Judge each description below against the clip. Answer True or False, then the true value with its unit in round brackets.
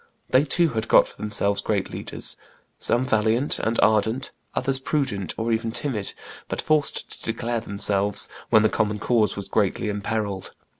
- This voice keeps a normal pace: True (160 wpm)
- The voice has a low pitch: True (110 Hz)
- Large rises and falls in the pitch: False (3.2 semitones)